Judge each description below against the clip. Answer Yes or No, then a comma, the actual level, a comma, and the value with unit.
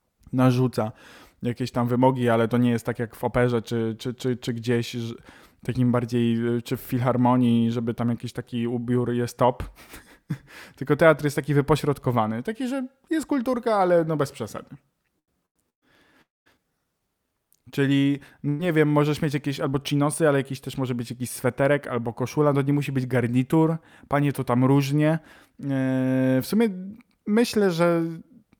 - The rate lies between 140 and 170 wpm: Yes, average, 155 wpm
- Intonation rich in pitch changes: No, average, 3.7 semitones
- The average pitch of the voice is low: Yes, low, 130 Hz